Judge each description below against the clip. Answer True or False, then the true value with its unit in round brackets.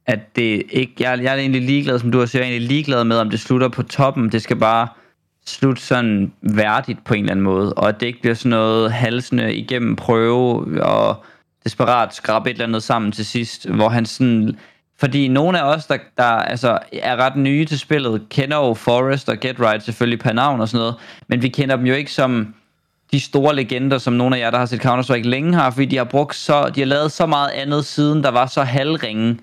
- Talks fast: True (235 wpm)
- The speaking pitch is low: True (125 Hz)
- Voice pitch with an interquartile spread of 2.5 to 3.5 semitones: True (3.0 semitones)